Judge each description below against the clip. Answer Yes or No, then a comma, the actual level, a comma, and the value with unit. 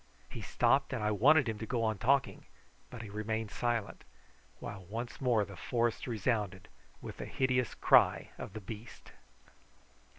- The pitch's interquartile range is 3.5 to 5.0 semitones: No, narrow, 2.6 semitones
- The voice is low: Yes, low, 115 Hz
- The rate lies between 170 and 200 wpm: No, average, 160 wpm